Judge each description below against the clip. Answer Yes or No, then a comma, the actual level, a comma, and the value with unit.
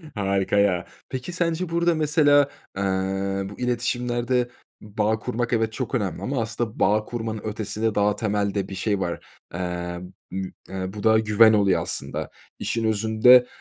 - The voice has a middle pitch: No, low, 110 Hz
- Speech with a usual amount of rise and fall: Yes, average, 3.5 semitones